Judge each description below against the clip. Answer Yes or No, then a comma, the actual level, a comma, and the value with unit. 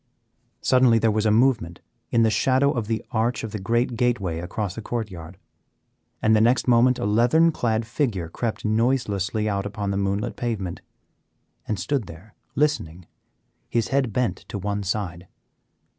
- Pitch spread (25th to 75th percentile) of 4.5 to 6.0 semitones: No, average, 3.4 semitones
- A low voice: Yes, low, 110 Hz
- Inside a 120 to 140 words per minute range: No, average, 165 wpm